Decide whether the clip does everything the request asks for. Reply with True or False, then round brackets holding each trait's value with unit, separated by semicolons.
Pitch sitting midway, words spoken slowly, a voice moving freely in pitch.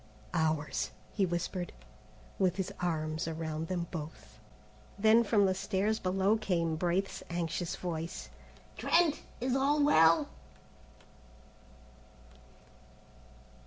False (180 Hz; 95 wpm; 3.8 semitones)